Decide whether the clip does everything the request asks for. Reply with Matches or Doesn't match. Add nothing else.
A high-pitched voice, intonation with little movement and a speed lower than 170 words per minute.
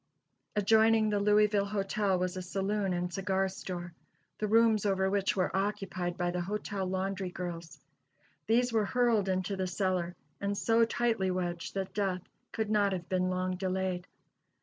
Matches